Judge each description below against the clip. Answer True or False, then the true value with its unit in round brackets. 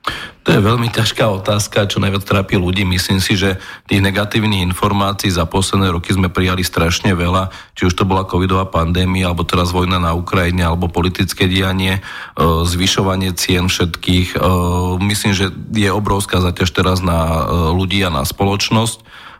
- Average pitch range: False (1.9 semitones)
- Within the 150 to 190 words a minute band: True (155 wpm)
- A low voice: True (95 Hz)